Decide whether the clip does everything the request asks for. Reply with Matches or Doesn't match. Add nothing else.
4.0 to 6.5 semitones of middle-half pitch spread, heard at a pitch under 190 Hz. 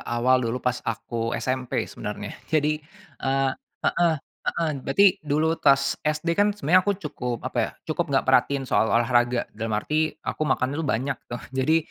Matches